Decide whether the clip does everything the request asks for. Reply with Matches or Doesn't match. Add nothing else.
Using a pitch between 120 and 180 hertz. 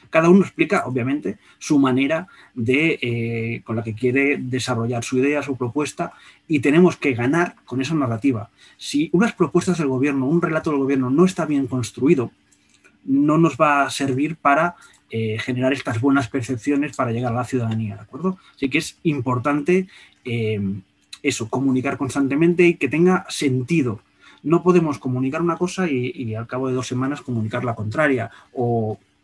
Matches